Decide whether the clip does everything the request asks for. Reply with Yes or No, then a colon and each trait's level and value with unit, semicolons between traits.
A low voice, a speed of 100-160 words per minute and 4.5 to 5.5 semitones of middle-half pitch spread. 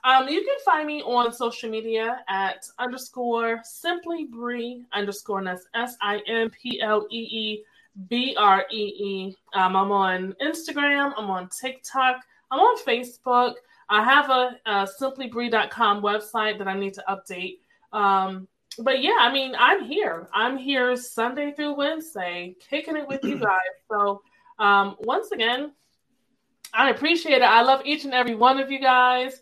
No: high, 240 Hz; slow, 135 wpm; average, 4.9 semitones